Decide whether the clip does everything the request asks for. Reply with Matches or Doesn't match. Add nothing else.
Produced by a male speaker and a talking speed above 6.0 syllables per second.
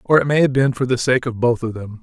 Matches